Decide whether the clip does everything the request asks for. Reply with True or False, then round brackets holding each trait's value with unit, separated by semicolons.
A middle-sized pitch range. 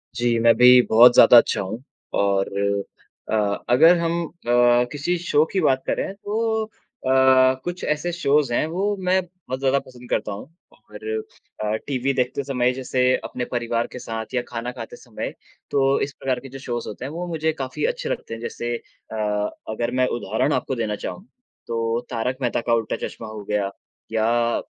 True (4.3 semitones)